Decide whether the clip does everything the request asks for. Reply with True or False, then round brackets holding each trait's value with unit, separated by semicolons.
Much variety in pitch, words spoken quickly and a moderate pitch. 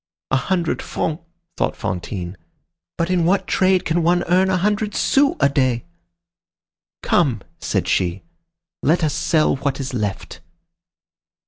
False (5.9 semitones; 135 wpm; 160 Hz)